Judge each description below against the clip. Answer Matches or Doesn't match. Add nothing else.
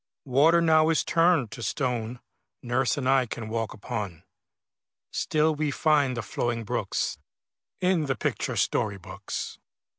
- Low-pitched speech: Matches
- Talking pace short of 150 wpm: Matches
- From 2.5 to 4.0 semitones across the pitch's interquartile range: Doesn't match